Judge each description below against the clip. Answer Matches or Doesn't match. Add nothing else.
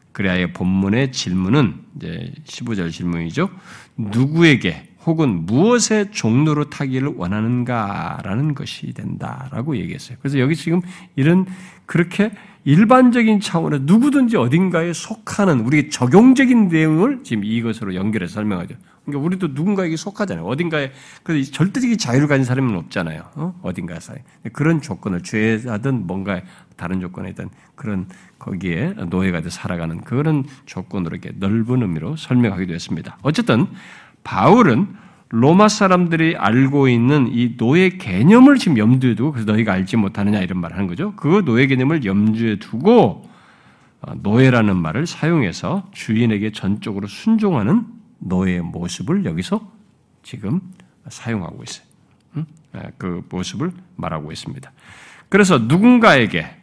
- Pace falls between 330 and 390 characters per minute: Matches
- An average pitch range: Doesn't match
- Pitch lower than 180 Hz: Matches